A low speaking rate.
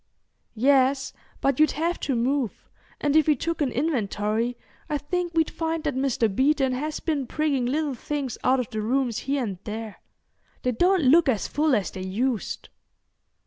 No: average, 175 wpm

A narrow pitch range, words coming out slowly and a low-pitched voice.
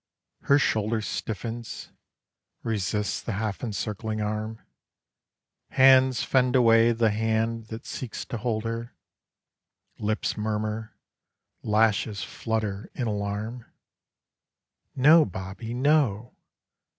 Yes: narrow, 1.9 semitones; slow, 95 wpm; low, 110 Hz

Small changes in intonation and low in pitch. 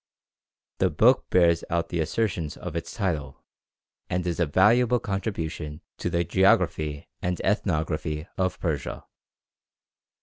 No: average, 3.2 semitones; very low, 85 Hz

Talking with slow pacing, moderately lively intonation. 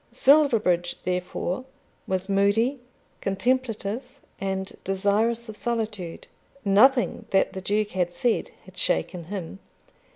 Yes: slow, 105 wpm; average, 3.5 semitones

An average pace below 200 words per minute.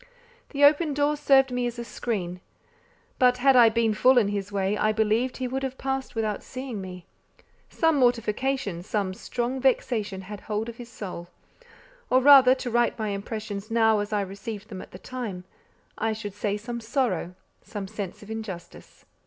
Yes: average, 180 wpm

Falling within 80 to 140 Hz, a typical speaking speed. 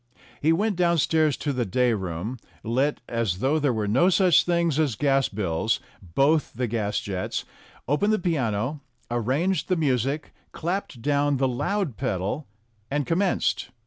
Yes: low, 135 Hz; average, 150 wpm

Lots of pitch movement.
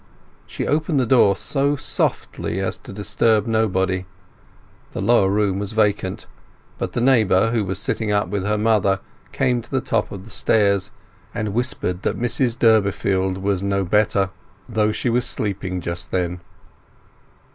No: average, 3.0 semitones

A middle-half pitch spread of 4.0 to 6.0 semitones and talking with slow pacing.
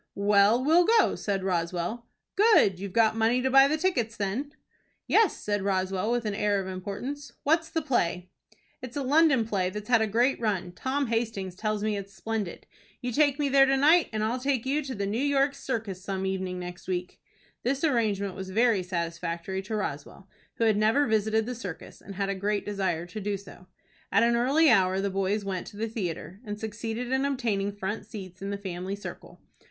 No: average, 4.6 semitones; fast, 205 wpm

